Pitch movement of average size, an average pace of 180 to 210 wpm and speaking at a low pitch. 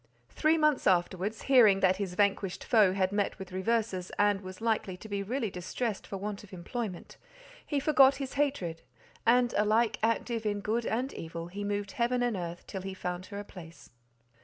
No: average, 3.9 semitones; average, 185 wpm; high, 205 Hz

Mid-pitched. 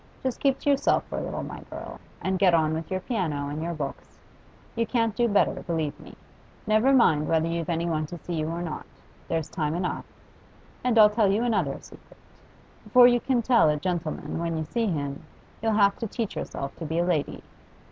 Yes: medium, 175 Hz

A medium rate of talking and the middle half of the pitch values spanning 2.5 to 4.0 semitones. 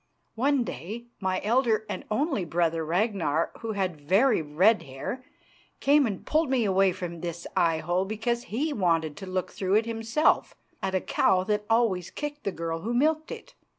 No: average, 175 wpm; wide, 5.4 semitones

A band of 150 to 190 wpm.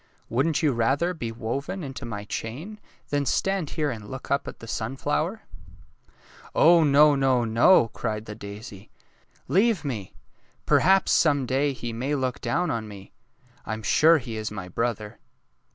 Yes: average, 175 wpm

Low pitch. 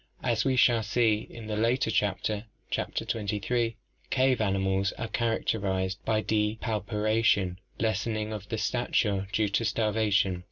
Yes: low, 110 Hz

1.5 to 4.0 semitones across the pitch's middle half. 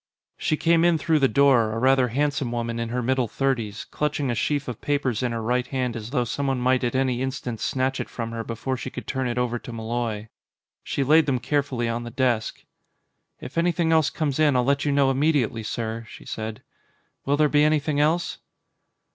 Yes: average, 3.4 semitones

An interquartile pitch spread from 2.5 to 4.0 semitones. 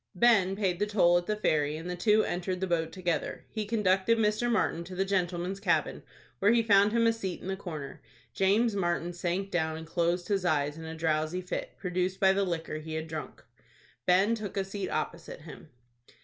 Yes: average, 3.1 semitones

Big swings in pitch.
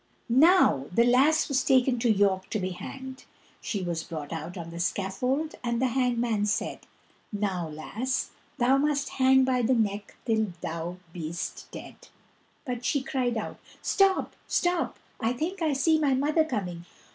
Yes: wide, 5.8 semitones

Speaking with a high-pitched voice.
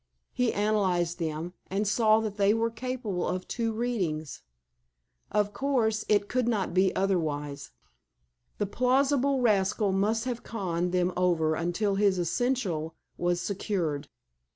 Yes: high, 200 Hz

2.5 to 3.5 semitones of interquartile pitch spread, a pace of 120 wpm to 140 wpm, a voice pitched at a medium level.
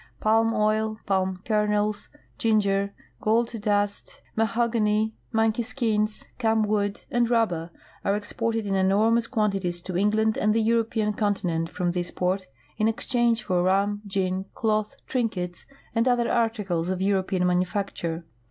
No: average, 2.8 semitones; slow, 135 wpm; high, 210 Hz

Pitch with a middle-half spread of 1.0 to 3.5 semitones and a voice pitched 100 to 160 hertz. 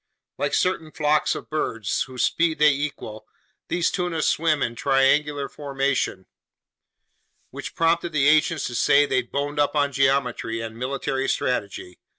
Yes: average, 3.1 semitones; medium, 140 Hz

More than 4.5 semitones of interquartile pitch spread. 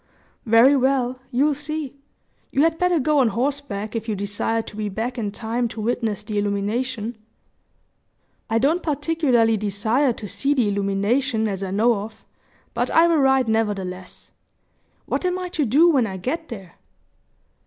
Yes: average, 5.1 semitones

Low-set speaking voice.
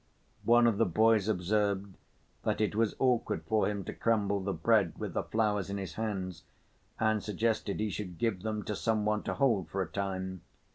Yes: low, 105 Hz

